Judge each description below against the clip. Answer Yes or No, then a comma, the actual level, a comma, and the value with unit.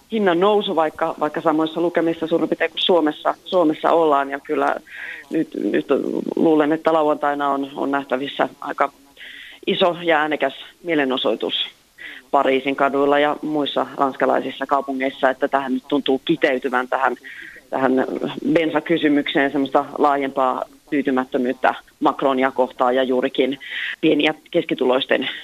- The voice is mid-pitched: Yes, medium, 145 Hz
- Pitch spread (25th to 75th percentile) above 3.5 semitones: No, average, 3.0 semitones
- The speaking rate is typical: Yes, average, 120 wpm